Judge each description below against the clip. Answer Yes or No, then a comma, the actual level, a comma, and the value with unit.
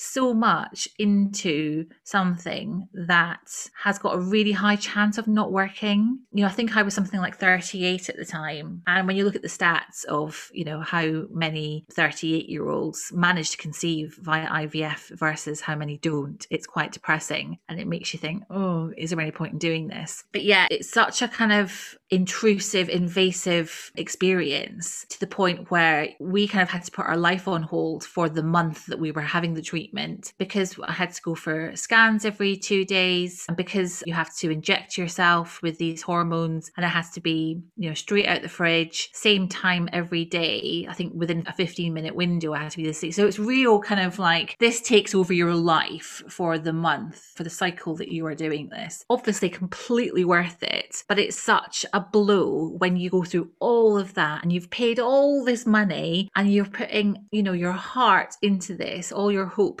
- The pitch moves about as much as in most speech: Yes, average, 3.5 semitones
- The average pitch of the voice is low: No, medium, 180 Hz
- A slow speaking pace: No, fast, 205 wpm